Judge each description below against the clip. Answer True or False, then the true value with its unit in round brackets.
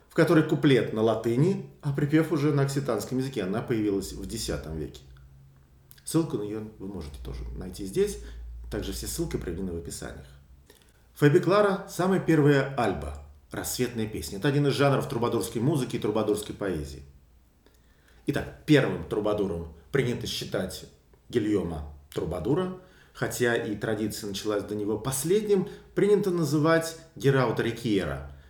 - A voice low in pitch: True (110 Hz)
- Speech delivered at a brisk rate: False (135 wpm)